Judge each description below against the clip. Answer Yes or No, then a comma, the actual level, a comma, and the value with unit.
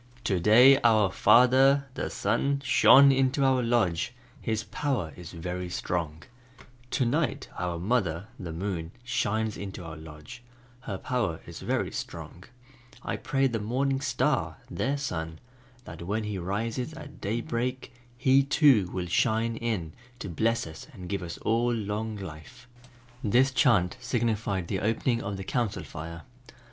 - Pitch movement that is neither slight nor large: No, wide, 5.9 semitones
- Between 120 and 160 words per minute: Yes, average, 140 wpm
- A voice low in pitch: Yes, low, 110 Hz